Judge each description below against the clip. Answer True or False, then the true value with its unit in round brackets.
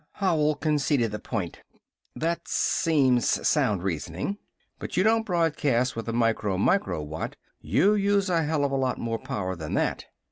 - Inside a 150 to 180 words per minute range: True (165 wpm)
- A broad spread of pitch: True (7.9 semitones)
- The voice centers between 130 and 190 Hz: True (135 Hz)